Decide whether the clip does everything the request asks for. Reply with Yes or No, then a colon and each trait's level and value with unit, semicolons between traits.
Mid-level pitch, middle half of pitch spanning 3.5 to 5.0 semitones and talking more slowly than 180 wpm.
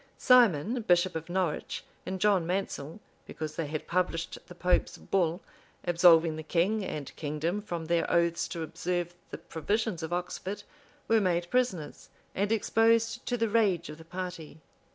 Yes: medium, 175 Hz; average, 3.9 semitones; average, 160 wpm